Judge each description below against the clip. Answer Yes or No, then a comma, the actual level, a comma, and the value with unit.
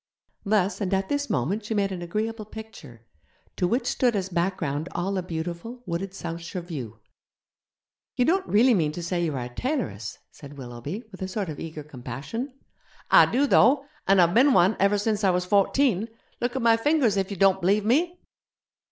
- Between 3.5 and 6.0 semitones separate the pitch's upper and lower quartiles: Yes, average, 5.0 semitones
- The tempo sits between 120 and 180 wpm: No, average, 190 wpm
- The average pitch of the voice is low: No, high, 195 Hz